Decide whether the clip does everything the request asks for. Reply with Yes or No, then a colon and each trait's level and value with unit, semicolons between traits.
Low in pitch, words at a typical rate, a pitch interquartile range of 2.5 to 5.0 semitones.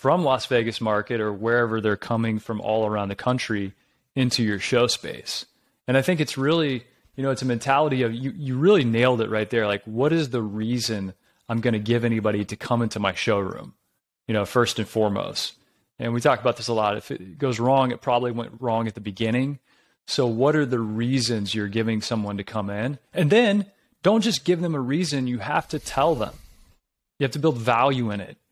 No: low, 120 Hz; fast, 220 wpm; average, 3.5 semitones